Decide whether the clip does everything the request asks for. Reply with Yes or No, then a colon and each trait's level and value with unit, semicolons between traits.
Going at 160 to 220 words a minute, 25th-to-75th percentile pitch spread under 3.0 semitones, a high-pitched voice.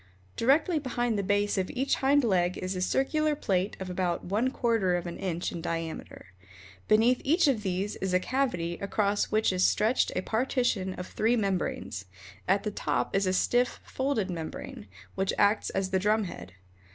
No: average, 180 wpm; average, 4.8 semitones; high, 200 Hz